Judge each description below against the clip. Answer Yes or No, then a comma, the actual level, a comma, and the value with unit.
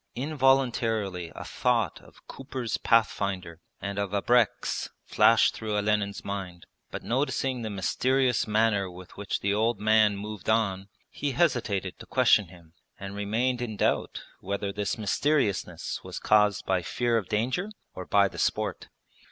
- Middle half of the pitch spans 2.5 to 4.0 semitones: Yes, average, 3.6 semitones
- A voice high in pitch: No, low, 105 Hz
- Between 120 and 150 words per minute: Yes, average, 145 wpm